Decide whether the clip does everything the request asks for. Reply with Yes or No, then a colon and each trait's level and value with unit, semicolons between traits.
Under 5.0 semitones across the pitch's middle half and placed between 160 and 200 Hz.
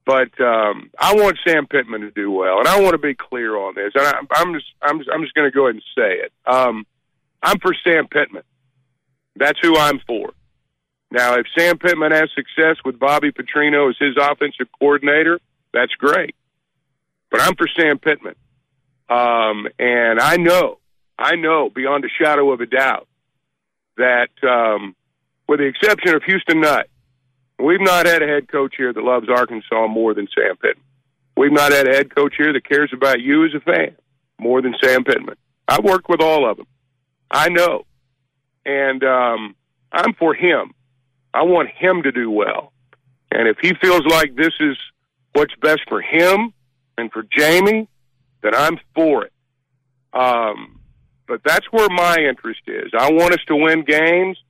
No: average, 3.8 semitones; medium, 140 Hz